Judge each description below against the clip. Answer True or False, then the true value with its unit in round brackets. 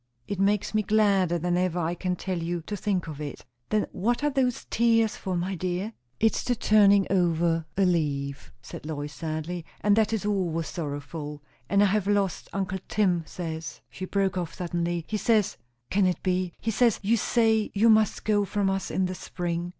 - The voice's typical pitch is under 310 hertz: True (185 Hz)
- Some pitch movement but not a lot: True (3.5 semitones)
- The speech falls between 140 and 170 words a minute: False (195 wpm)